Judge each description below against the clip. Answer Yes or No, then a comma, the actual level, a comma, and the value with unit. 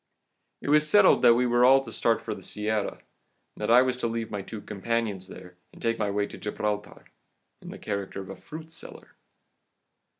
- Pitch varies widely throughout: No, average, 3.4 semitones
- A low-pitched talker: Yes, low, 115 Hz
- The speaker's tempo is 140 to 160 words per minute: No, average, 200 wpm